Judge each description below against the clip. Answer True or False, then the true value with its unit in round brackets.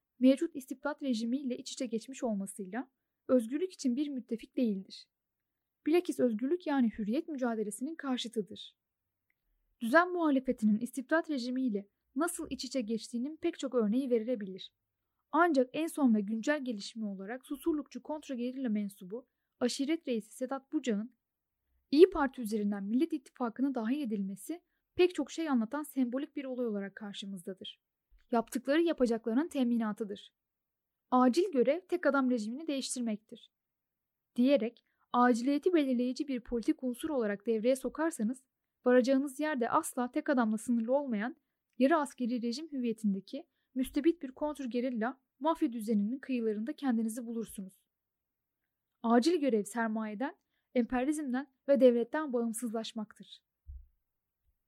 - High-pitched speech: True (255 Hz)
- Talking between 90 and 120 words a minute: True (115 wpm)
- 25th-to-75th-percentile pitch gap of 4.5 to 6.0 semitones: False (3.9 semitones)